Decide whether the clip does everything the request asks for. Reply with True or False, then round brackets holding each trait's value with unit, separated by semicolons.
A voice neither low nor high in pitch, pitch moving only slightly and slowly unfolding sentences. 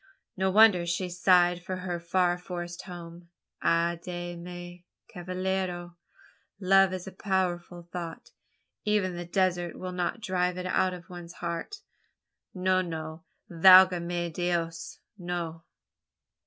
True (175 Hz; 1.2 semitones; 130 wpm)